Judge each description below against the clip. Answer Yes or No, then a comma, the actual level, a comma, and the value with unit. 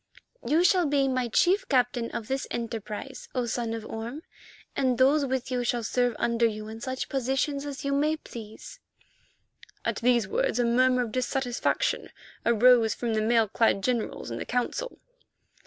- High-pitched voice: Yes, high, 245 Hz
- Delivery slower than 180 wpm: Yes, average, 170 wpm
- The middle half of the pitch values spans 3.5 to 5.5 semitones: No, average, 2.8 semitones